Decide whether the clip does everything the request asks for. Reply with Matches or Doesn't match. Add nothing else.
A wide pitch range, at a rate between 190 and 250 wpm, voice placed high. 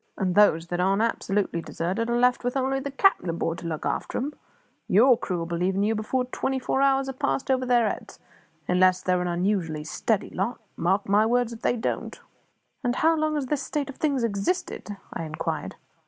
Matches